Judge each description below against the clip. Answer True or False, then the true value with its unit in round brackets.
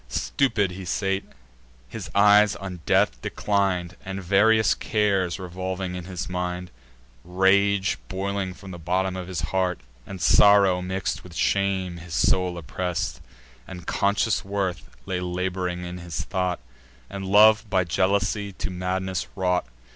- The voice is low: True (95 Hz)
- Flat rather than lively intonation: True (1.7 semitones)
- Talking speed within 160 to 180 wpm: False (140 wpm)